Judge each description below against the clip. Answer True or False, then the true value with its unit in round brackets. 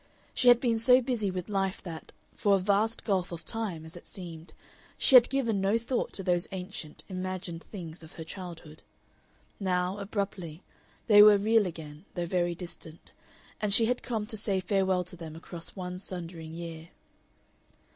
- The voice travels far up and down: False (3.5 semitones)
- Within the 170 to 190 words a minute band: True (175 wpm)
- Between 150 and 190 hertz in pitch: True (185 Hz)